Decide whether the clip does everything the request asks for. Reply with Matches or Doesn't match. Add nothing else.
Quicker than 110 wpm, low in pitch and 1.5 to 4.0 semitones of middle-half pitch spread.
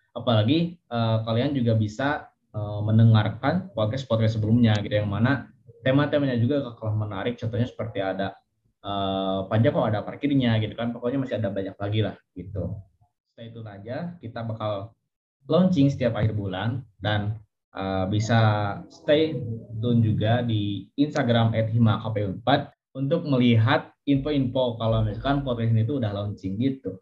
Matches